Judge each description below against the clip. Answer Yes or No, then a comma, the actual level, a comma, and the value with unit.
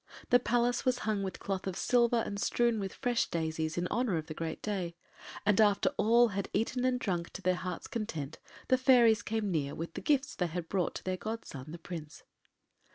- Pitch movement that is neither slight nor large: No, wide, 5.7 semitones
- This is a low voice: No, high, 200 Hz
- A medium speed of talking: No, fast, 210 wpm